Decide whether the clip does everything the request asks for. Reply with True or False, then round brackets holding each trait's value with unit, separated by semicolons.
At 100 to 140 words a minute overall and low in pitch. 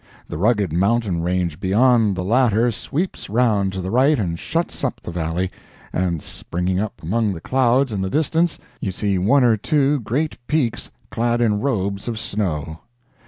False (170 wpm; 105 Hz)